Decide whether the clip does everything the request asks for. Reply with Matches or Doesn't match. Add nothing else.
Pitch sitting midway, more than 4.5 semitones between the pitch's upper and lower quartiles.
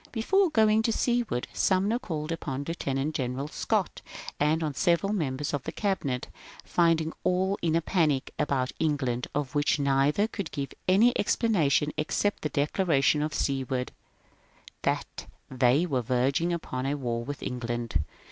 Matches